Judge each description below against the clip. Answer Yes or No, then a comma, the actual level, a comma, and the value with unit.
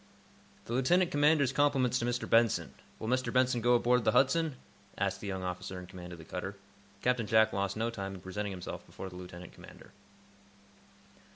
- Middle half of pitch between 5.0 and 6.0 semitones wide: Yes, average, 5.3 semitones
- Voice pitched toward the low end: Yes, low, 115 Hz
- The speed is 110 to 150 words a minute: No, average, 185 wpm